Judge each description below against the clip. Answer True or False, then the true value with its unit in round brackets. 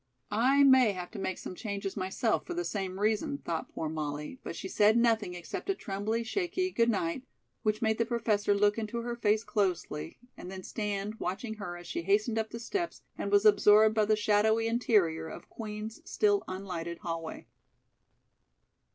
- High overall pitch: True (215 Hz)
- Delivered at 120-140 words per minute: False (180 wpm)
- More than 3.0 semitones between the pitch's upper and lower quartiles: True (3.5 semitones)